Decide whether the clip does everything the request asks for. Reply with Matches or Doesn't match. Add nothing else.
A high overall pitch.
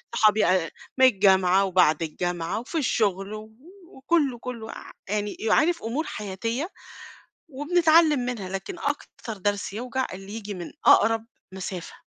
Matches